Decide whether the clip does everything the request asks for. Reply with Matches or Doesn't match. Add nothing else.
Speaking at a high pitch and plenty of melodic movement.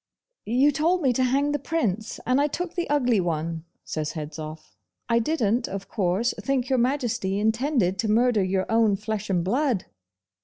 Matches